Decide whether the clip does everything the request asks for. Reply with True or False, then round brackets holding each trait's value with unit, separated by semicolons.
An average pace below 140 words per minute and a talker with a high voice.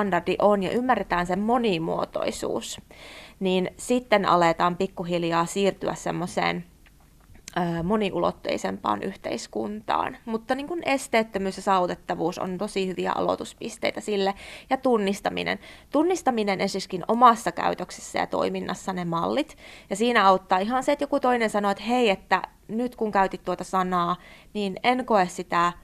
True (130 wpm; 195 Hz)